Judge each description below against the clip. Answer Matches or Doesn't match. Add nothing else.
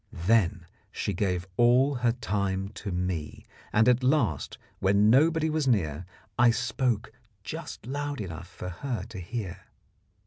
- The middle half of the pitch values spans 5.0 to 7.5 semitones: Matches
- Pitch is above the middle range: Doesn't match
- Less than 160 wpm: Matches